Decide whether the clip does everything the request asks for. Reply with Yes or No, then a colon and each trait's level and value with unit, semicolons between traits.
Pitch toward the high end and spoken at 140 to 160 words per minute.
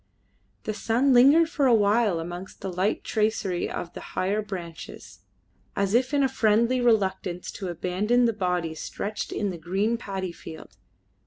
Yes: high, 205 Hz; average, 155 wpm